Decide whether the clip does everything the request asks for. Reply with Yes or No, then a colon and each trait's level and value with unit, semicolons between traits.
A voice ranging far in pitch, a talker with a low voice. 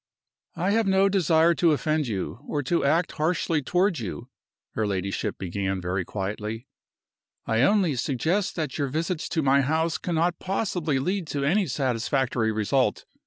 No: wide, 7.0 semitones; medium, 150 Hz